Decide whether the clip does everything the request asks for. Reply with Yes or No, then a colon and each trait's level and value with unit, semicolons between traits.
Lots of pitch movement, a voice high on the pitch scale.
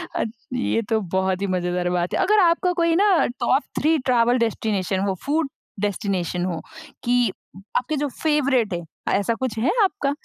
Yes: wide, 7.9 semitones; high, 235 Hz